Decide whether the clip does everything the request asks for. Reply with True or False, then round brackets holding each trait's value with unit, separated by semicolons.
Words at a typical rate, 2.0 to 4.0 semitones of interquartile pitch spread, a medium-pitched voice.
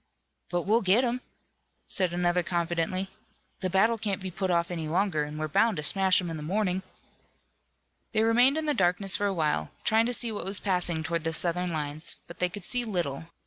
False (210 wpm; 3.6 semitones; 180 Hz)